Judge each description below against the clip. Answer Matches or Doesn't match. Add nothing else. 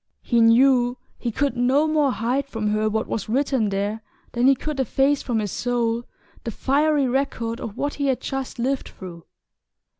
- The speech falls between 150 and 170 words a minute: Doesn't match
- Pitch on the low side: Doesn't match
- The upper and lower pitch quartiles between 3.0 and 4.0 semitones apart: Matches